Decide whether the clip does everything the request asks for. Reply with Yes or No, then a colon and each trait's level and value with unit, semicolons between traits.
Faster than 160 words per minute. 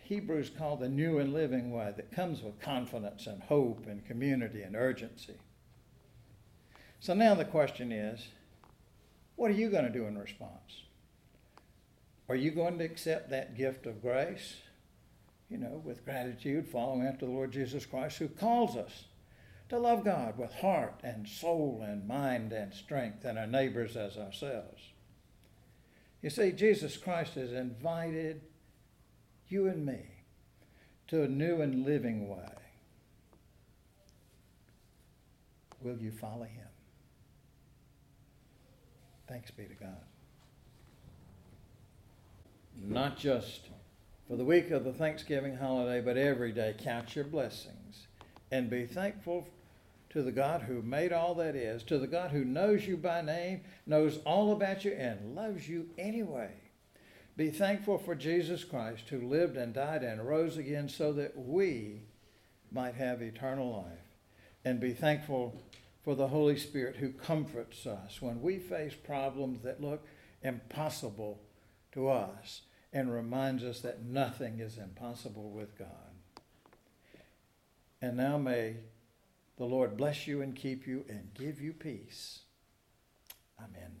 No: average, 140 wpm